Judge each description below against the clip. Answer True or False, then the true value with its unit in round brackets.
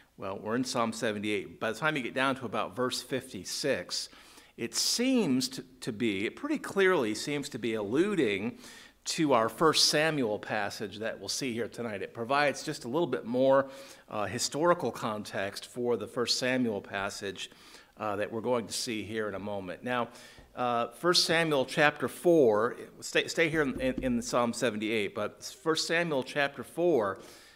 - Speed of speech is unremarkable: True (175 wpm)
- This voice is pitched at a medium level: False (125 Hz)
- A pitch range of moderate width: False (5.7 semitones)